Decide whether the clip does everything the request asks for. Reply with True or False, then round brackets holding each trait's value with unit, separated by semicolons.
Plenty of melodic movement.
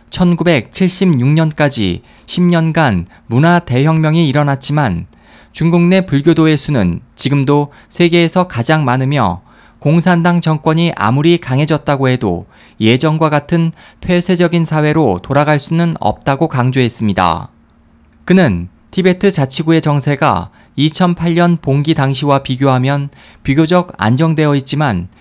False (4.9 semitones)